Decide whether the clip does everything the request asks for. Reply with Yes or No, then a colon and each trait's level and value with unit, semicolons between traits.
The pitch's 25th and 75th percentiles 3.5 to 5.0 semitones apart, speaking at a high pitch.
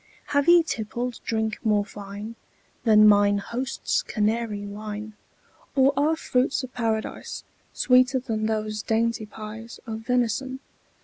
No: average, 2.9 semitones; high, 225 Hz